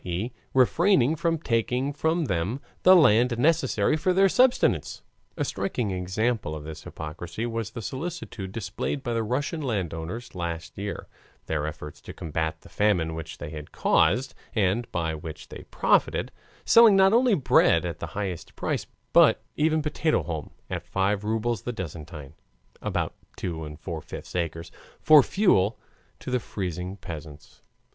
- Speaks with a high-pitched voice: No, low, 105 Hz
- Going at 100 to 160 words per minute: Yes, average, 155 wpm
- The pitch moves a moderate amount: No, wide, 8.5 semitones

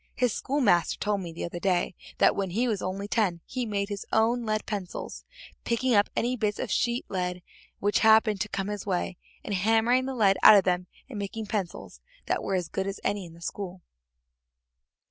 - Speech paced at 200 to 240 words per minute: Yes, fast, 205 wpm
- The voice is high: Yes, high, 205 Hz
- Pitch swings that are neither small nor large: Yes, average, 3.1 semitones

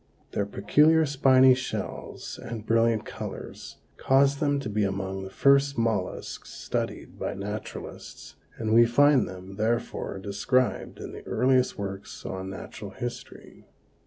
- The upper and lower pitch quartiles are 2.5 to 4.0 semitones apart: No, average, 5.0 semitones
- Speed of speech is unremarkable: No, slow, 130 wpm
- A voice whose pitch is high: No, low, 115 Hz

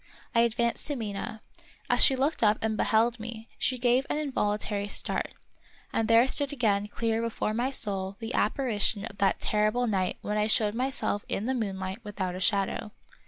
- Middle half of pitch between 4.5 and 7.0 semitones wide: No, average, 2.8 semitones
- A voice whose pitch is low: No, high, 220 Hz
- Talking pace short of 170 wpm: No, average, 185 wpm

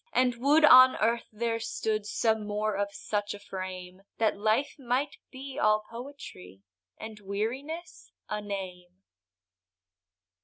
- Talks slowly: Yes, slow, 125 wpm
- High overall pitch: Yes, high, 215 Hz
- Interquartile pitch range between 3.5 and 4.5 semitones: Yes, average, 4.0 semitones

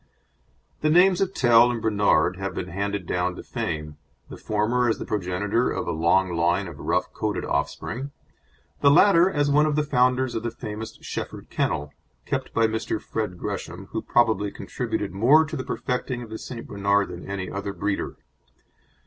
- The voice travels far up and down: No, average, 5.0 semitones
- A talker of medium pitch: No, low, 110 Hz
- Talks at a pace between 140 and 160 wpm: No, average, 180 wpm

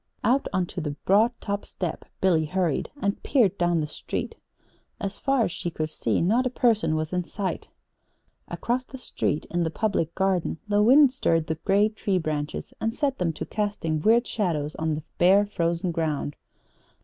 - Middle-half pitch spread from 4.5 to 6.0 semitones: Yes, average, 5.1 semitones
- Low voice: No, medium, 185 Hz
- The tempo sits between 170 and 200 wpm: Yes, average, 185 wpm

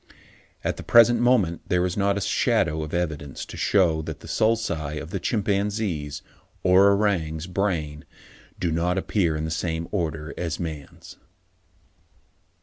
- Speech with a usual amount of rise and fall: Yes, average, 4.2 semitones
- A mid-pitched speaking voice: No, very low, 85 Hz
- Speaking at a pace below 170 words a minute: Yes, average, 150 wpm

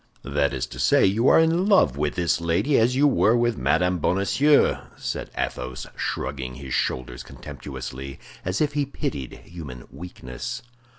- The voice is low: Yes, very low, 85 Hz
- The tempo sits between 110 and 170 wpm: Yes, average, 160 wpm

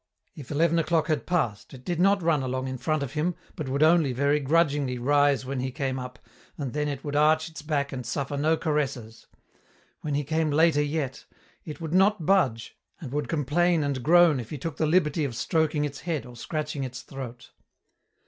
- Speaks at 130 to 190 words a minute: No, fast, 205 wpm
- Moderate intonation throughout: Yes, average, 3.2 semitones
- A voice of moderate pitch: Yes, medium, 145 Hz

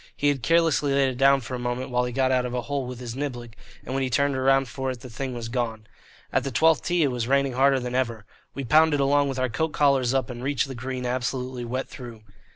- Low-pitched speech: Yes, low, 130 Hz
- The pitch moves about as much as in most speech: No, narrow, 2.0 semitones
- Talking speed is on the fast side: Yes, fast, 265 wpm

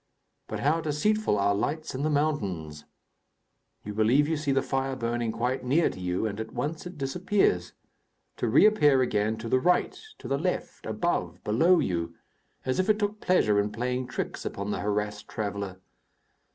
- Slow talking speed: No, average, 175 wpm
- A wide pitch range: Yes, wide, 6.9 semitones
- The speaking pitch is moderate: No, low, 125 Hz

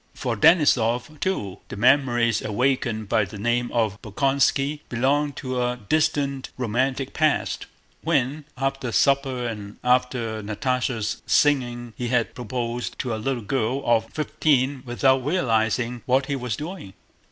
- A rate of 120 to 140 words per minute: Yes, slow, 135 wpm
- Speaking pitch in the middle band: No, low, 125 Hz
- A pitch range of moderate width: Yes, average, 3.1 semitones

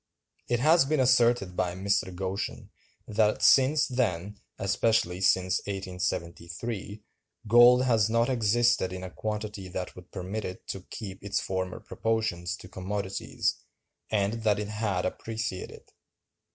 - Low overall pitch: Yes, low, 100 Hz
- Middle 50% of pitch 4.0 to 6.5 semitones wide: No, average, 3.5 semitones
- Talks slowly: Yes, slow, 130 wpm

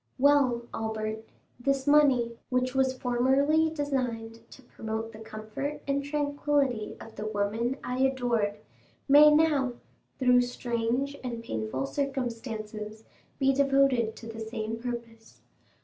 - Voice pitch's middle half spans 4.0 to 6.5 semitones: No, average, 3.5 semitones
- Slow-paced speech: Yes, slow, 120 wpm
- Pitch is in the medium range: No, high, 245 Hz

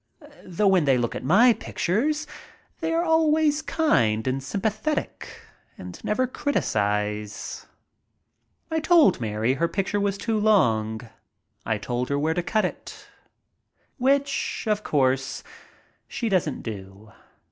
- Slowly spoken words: Yes, slow, 125 wpm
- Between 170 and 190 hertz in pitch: Yes, medium, 185 Hz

